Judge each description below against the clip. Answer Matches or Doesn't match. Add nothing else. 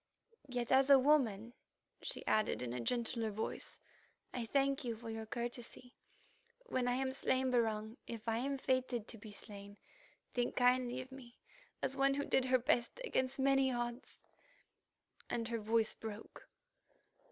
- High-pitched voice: Matches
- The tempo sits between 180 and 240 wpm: Doesn't match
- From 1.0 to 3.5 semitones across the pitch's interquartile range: Matches